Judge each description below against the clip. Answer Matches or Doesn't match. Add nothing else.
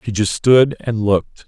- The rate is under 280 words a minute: Matches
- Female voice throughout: Doesn't match